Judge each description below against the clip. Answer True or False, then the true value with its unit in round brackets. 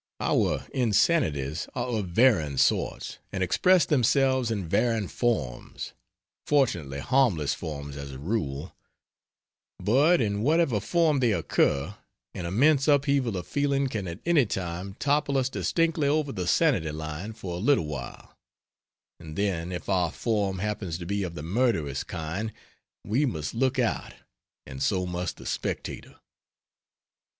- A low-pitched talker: True (105 Hz)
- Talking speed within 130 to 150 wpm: True (140 wpm)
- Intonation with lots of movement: True (7.8 semitones)